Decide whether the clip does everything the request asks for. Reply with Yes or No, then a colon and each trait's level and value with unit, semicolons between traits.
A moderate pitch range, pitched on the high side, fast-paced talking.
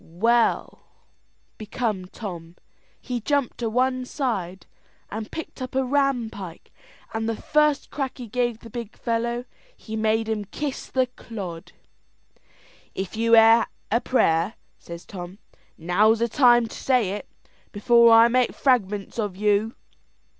No: average, 3.4 semitones; high, 225 Hz; average, 145 wpm